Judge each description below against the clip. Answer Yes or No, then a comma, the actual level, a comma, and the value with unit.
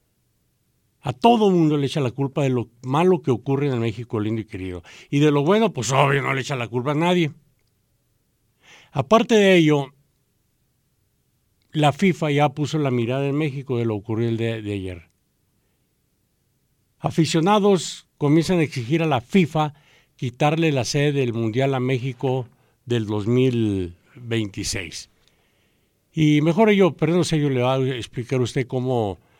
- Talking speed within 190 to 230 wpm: No, average, 160 wpm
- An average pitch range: Yes, average, 4.7 semitones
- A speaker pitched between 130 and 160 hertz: Yes, low, 135 Hz